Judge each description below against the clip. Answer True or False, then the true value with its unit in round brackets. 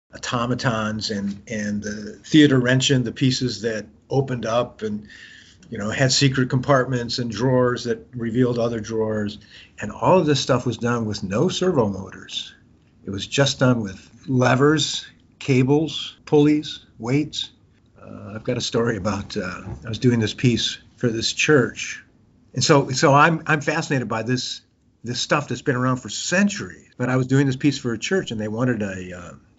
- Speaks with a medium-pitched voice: False (120 Hz)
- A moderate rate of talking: True (175 wpm)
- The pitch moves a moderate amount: True (3.8 semitones)